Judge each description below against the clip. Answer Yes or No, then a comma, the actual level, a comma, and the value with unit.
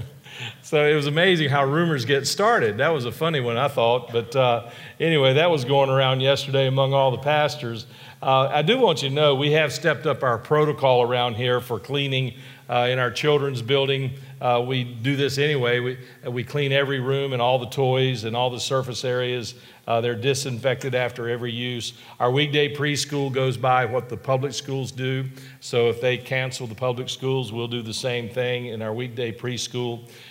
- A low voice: Yes, low, 130 Hz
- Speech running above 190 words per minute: Yes, average, 200 wpm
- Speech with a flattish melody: Yes, narrow, 2.3 semitones